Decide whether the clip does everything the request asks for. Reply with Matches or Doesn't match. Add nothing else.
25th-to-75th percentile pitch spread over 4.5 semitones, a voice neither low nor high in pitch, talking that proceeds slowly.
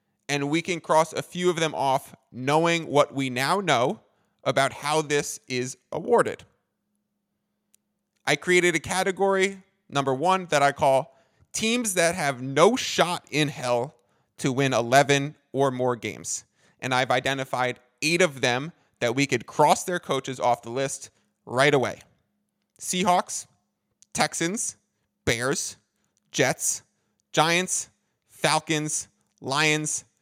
Matches